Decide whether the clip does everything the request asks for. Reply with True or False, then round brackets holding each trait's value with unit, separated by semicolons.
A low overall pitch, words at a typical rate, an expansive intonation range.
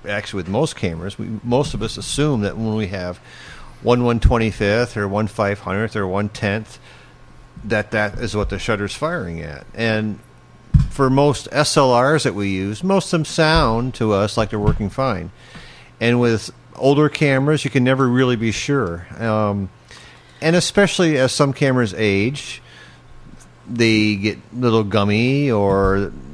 False (110 Hz; 150 wpm; 4.6 semitones)